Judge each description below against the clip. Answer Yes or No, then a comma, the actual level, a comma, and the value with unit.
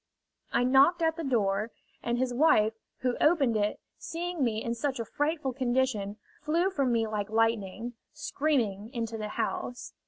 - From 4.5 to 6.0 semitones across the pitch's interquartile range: Yes, average, 4.9 semitones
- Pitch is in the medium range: No, high, 245 Hz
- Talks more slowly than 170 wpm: Yes, average, 160 wpm